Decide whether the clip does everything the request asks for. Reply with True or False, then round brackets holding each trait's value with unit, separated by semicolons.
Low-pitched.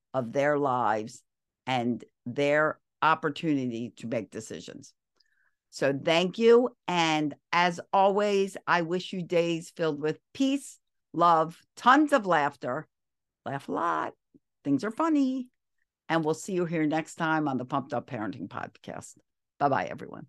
False (160 Hz)